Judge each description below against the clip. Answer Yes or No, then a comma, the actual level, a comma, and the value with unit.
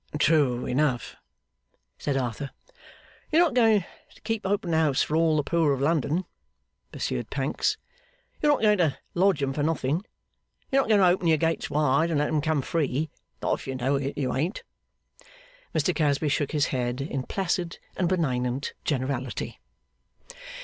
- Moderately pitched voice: Yes, medium, 150 Hz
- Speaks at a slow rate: No, average, 165 wpm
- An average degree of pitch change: Yes, average, 4.1 semitones